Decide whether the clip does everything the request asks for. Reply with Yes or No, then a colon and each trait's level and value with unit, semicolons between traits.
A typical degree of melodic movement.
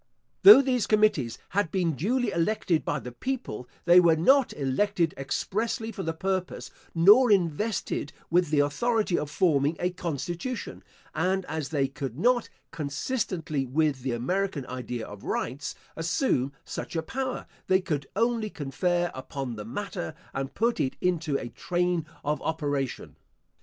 No: wide, 6.3 semitones